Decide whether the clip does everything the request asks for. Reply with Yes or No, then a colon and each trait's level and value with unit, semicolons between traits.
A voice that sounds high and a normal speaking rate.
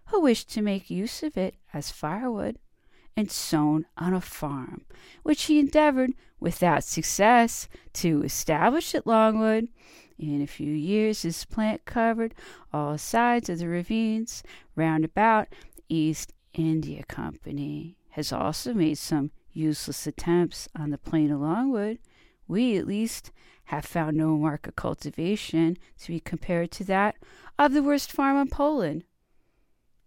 No: medium, 180 Hz; average, 145 wpm